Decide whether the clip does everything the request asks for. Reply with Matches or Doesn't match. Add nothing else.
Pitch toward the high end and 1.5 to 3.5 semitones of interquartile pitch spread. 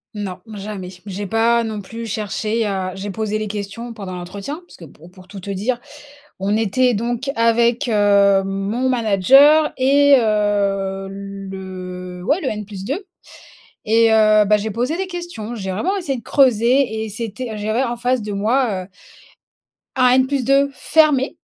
Doesn't match